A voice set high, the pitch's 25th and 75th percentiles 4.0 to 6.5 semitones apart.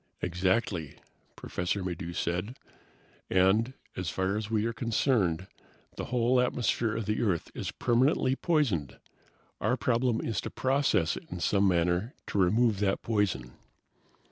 No: low, 105 Hz; average, 4.9 semitones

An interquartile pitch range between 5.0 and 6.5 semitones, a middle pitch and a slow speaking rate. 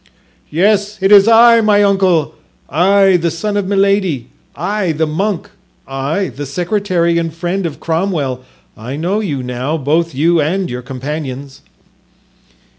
Yes: wide, 5.5 semitones; medium, 170 Hz; slow, 120 wpm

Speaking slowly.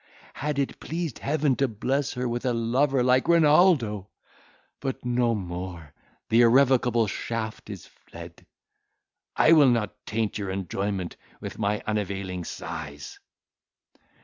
Yes: slow, 125 wpm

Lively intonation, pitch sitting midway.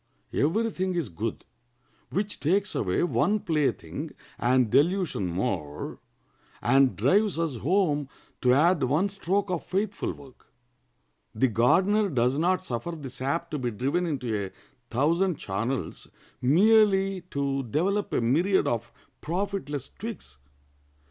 Yes: wide, 7.1 semitones; medium, 155 Hz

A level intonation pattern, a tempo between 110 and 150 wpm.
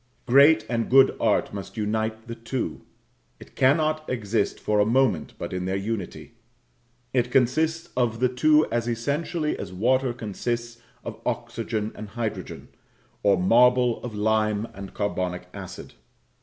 No: average, 3.4 semitones; average, 140 wpm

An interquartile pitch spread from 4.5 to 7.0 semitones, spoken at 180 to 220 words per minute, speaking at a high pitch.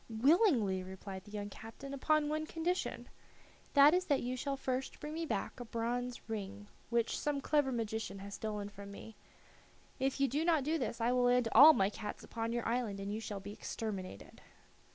Yes: average, 5.1 semitones; average, 195 wpm; high, 235 Hz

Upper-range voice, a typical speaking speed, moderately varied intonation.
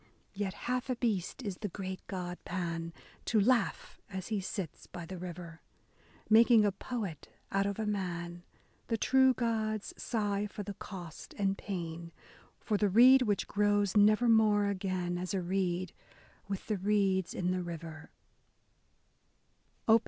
Yes: high, 195 Hz; average, 150 wpm; average, 3.1 semitones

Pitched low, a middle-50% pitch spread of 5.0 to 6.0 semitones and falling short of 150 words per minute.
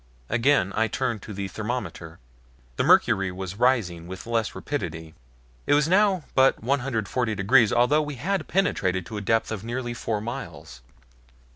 No: low, 115 Hz; wide, 5.4 semitones; average, 155 wpm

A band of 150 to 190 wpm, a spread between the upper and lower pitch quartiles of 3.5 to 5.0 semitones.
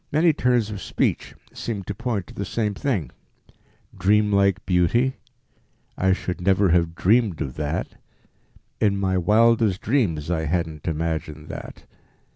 No: slow, 135 wpm; average, 4.6 semitones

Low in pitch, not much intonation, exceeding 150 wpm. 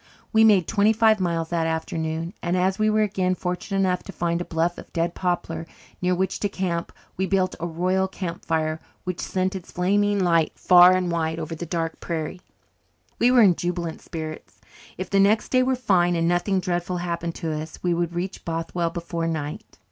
No: medium, 175 Hz; narrow, 2.3 semitones; average, 200 wpm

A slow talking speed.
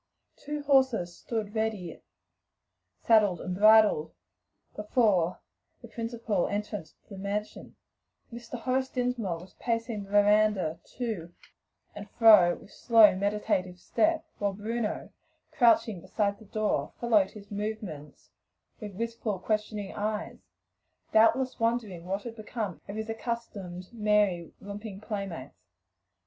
Yes: slow, 125 wpm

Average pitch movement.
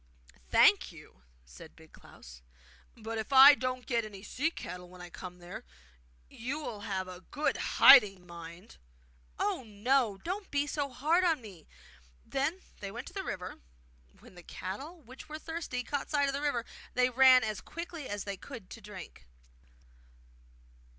No: wide, 6.9 semitones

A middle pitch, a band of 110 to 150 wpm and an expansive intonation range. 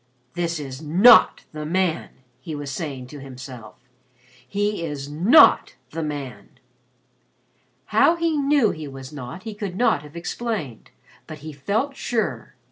Yes: medium, 160 Hz; average, 140 wpm; wide, 6.7 semitones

